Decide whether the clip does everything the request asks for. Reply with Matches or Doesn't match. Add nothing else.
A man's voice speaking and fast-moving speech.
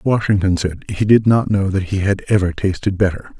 Matches